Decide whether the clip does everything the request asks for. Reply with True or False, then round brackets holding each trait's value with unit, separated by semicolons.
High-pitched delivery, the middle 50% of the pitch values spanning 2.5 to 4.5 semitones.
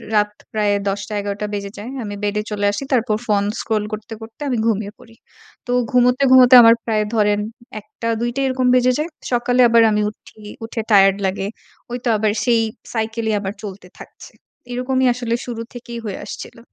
True (225 Hz; 2.8 semitones)